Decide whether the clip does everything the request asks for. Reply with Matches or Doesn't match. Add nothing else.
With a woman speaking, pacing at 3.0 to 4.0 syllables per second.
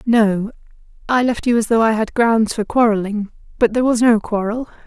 Doesn't match